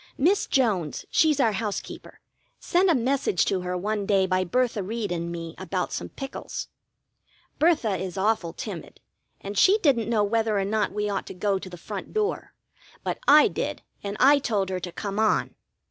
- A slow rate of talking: No, average, 185 wpm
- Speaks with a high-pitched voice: Yes, high, 210 Hz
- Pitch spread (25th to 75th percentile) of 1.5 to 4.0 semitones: No, average, 5.1 semitones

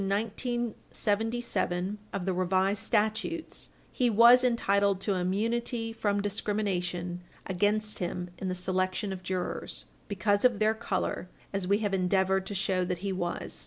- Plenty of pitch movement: No, average, 2.8 semitones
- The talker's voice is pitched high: Yes, high, 200 Hz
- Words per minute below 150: Yes, average, 140 wpm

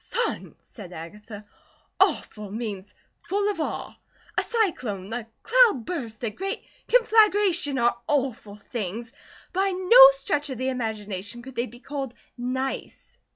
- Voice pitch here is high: Yes, very high, 255 Hz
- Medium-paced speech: No, slow, 130 wpm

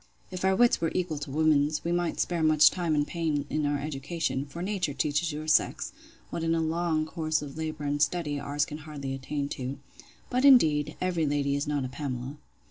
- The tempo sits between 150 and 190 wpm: No, fast, 205 wpm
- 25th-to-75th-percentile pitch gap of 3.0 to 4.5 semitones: No, narrow, 2.5 semitones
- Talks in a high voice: No, medium, 155 Hz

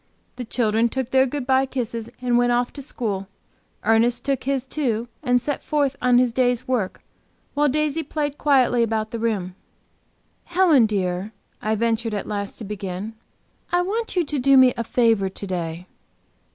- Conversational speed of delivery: Yes, average, 175 wpm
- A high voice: Yes, high, 245 Hz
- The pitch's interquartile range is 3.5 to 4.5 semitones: Yes, average, 3.8 semitones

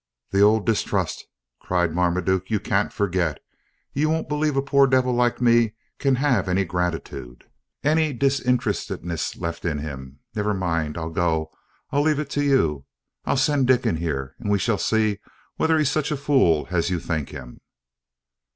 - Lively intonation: Yes, wide, 8.2 semitones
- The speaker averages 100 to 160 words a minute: No, average, 170 wpm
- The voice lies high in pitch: No, low, 105 Hz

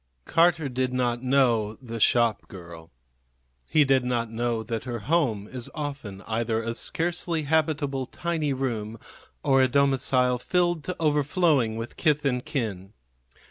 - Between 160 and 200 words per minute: No, average, 140 wpm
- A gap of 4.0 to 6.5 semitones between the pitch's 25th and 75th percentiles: Yes, average, 4.3 semitones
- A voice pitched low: Yes, low, 130 Hz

